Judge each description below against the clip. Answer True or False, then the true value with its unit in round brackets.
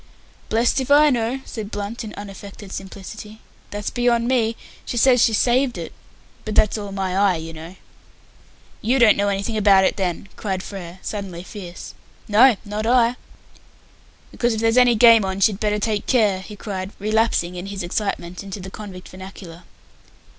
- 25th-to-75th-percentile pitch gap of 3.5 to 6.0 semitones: False (3.1 semitones)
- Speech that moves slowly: False (170 wpm)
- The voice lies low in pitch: False (205 Hz)